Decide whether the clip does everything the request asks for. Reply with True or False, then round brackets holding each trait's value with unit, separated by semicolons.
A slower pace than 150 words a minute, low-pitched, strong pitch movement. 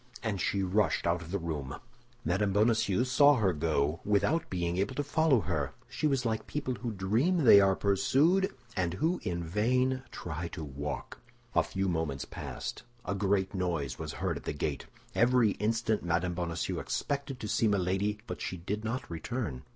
False (180 wpm; 100 Hz; 6.0 semitones)